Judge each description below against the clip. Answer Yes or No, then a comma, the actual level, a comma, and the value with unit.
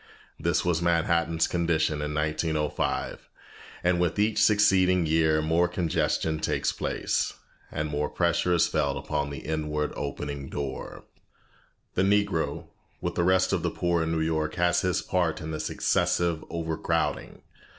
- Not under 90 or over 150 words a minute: Yes, average, 145 wpm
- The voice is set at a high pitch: No, very low, 80 Hz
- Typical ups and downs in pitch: No, narrow, 2.3 semitones